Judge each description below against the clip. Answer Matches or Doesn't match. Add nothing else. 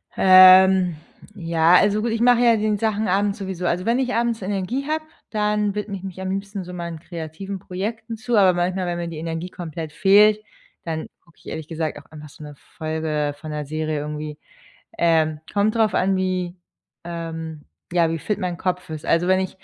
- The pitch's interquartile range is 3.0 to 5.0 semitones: Matches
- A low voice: Doesn't match